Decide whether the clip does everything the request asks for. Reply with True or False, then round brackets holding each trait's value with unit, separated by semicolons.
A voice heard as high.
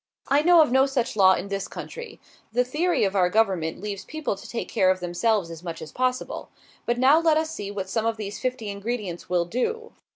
True (220 Hz)